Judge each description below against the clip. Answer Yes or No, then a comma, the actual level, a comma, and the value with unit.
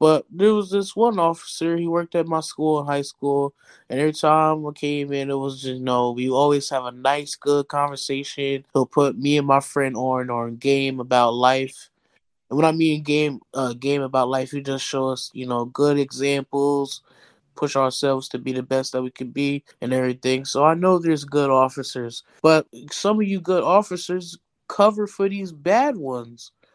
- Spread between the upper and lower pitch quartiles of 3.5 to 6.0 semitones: No, average, 3.0 semitones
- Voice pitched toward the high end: No, medium, 140 Hz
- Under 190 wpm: No, average, 200 wpm